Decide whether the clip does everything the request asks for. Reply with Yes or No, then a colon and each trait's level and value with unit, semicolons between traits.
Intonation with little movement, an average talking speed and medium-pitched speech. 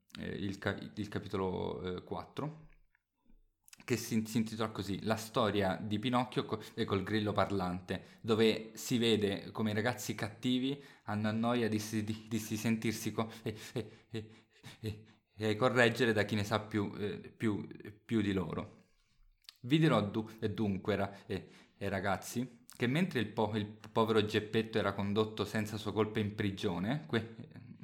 No: narrow, 1.8 semitones; average, 160 wpm; low, 110 Hz